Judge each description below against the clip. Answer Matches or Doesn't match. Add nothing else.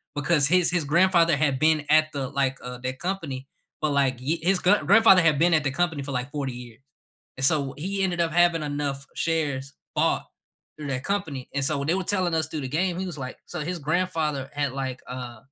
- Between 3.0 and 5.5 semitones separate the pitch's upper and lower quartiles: Matches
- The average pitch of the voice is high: Doesn't match